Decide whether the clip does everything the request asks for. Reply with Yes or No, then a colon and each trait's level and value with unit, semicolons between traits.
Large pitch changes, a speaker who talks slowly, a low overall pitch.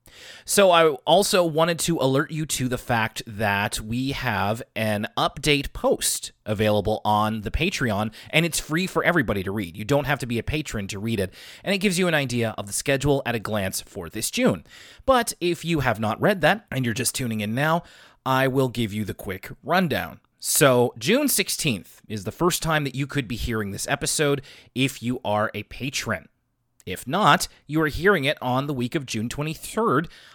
No: wide, 6.1 semitones; fast, 205 wpm; low, 130 Hz